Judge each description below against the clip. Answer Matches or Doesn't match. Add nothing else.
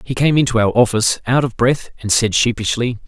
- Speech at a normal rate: Doesn't match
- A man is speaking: Matches